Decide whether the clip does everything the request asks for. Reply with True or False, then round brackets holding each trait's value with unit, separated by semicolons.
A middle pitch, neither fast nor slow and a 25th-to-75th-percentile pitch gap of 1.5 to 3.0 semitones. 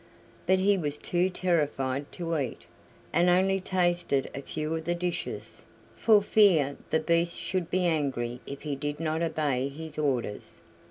False (160 Hz; 160 wpm; 3.8 semitones)